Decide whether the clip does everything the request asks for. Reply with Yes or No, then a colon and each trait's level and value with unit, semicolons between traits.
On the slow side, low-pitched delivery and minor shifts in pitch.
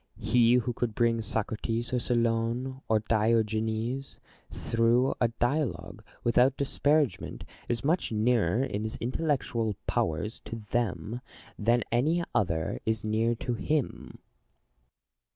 Yes: slow, 115 wpm; low, 115 Hz; narrow, 2.1 semitones